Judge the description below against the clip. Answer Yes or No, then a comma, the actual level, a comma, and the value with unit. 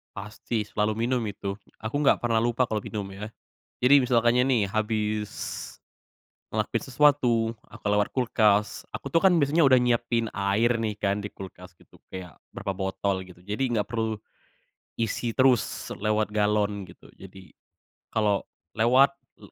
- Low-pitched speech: Yes, low, 110 Hz